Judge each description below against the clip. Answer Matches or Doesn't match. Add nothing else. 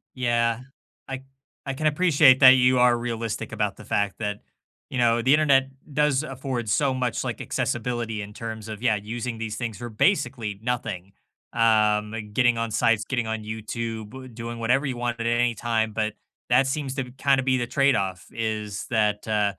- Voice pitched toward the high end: Doesn't match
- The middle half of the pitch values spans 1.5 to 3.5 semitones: Matches